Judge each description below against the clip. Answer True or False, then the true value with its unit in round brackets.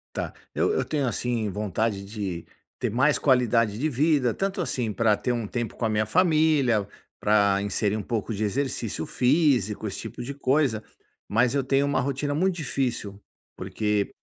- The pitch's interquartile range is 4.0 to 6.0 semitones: True (5.0 semitones)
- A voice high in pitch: False (120 Hz)